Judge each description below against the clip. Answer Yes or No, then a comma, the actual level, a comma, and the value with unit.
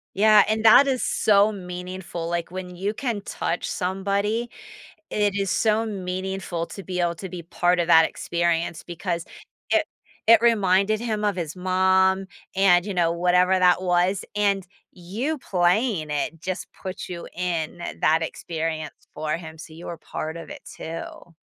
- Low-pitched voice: No, medium, 180 Hz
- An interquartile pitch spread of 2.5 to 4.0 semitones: Yes, average, 2.8 semitones